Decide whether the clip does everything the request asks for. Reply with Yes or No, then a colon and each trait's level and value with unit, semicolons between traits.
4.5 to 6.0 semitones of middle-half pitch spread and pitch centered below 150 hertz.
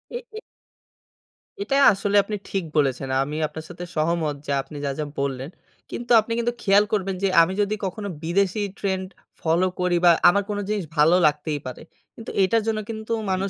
No: average, 4.9 semitones; medium, 185 Hz